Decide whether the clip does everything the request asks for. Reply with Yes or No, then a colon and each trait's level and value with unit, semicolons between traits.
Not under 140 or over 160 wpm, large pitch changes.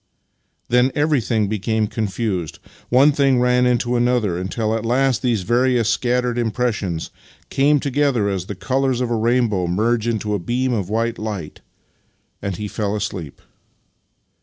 No: average, 155 wpm; average, 3.3 semitones